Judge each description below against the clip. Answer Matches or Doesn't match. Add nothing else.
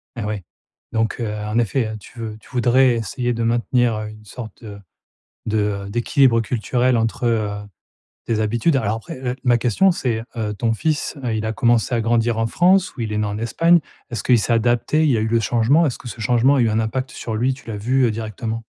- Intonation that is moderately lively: Doesn't match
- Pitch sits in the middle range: Doesn't match